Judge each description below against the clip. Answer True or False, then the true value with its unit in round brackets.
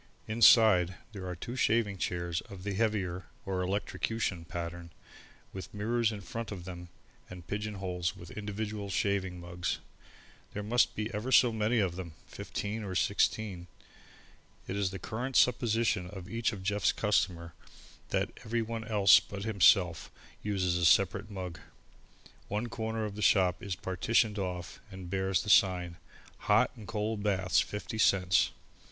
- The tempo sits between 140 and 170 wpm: True (150 wpm)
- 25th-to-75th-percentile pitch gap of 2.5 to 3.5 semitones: True (3.1 semitones)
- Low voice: True (100 Hz)